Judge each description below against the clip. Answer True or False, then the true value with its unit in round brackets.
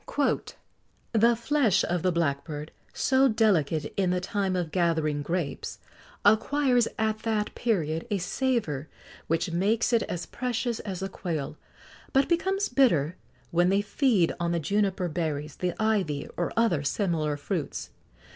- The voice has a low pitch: False (185 Hz)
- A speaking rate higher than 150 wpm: False (140 wpm)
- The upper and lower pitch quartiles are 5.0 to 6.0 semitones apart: True (5.6 semitones)